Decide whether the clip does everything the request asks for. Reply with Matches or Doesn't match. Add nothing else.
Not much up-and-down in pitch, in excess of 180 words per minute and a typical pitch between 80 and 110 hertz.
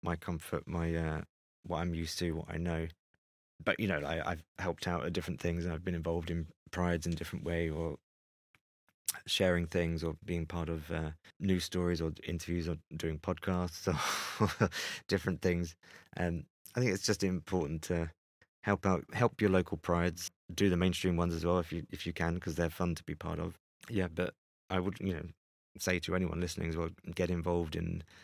Matches